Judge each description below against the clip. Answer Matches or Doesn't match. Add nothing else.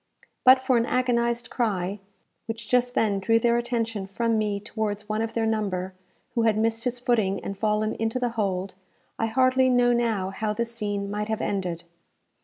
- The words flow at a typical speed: Matches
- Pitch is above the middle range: Matches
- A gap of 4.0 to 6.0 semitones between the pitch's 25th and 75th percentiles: Doesn't match